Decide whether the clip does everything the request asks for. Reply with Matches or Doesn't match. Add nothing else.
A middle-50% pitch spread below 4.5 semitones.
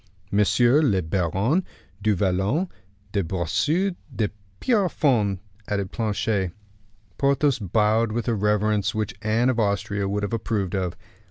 Matches